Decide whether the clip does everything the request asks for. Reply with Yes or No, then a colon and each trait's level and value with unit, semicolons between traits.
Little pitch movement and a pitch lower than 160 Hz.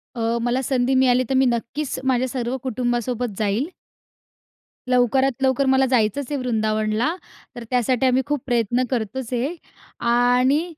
No: narrow, 1.9 semitones; very high, 250 Hz